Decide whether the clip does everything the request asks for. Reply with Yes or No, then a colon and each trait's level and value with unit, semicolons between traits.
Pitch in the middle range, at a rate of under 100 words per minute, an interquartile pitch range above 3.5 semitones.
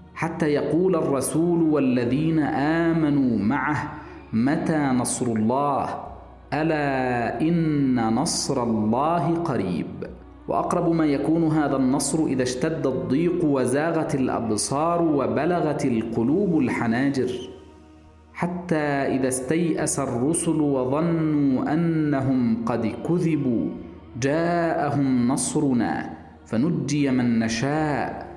Yes: medium, 145 Hz; average, 85 wpm; average, 4.1 semitones